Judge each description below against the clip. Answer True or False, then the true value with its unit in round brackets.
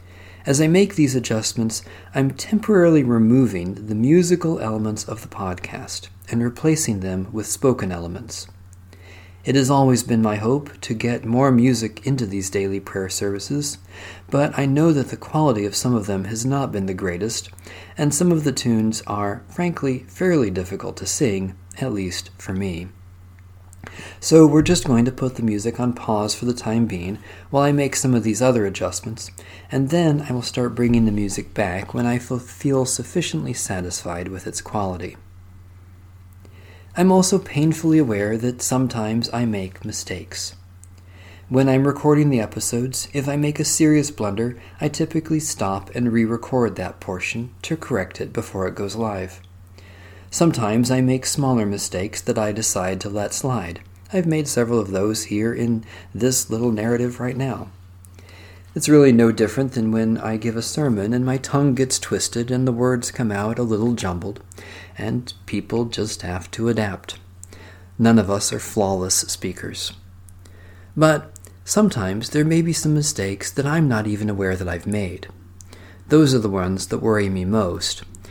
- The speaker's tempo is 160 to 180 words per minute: True (170 wpm)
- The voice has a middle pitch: False (110 Hz)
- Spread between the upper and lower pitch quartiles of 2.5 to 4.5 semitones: False (5.5 semitones)